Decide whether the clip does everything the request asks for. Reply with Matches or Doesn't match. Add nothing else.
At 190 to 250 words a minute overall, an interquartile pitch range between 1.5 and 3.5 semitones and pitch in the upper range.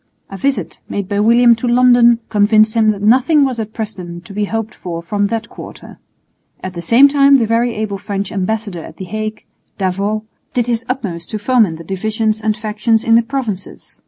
Matches